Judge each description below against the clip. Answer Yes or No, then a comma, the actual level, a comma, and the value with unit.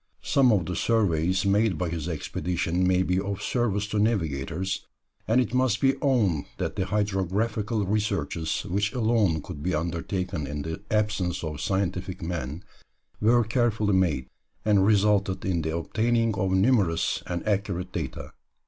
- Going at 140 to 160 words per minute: Yes, average, 150 wpm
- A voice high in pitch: No, very low, 95 Hz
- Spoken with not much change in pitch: No, average, 3.7 semitones